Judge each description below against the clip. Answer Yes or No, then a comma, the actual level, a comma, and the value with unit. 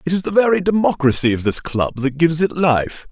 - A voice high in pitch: No, medium, 155 Hz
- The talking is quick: Yes, fast, 230 wpm